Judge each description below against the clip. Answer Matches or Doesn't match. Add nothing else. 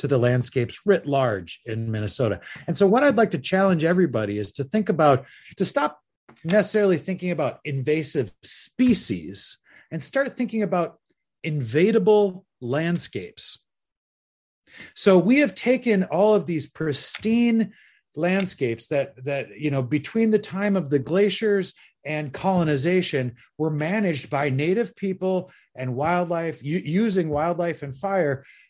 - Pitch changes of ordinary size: Doesn't match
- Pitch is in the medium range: Matches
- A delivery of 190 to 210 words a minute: Doesn't match